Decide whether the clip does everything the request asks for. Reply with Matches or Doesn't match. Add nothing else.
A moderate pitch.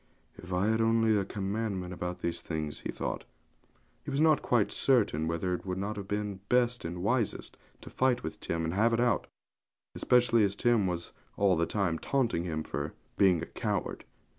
Doesn't match